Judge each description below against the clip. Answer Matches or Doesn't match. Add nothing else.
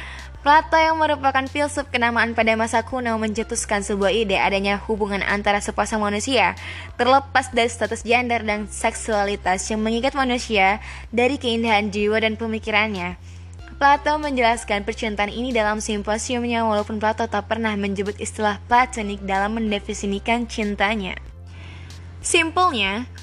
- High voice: Matches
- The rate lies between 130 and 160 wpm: Doesn't match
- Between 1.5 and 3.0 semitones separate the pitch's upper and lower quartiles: Matches